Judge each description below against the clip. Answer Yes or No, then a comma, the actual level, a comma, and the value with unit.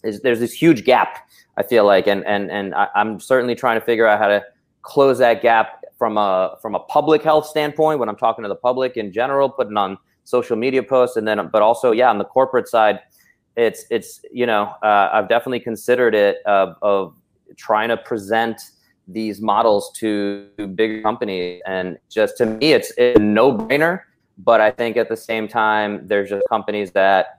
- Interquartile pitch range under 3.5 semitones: No, average, 4.0 semitones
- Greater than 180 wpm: Yes, average, 200 wpm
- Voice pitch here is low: Yes, low, 115 Hz